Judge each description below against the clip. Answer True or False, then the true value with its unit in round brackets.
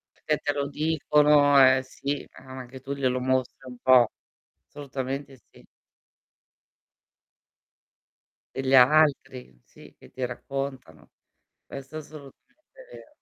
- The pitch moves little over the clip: True (2.0 semitones)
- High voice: False (135 Hz)